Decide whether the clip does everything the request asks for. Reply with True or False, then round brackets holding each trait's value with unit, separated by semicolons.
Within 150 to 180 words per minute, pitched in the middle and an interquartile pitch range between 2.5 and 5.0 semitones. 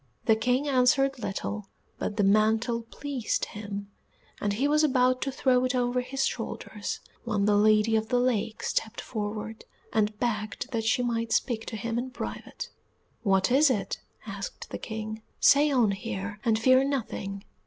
False (165 wpm; 225 Hz; 3.2 semitones)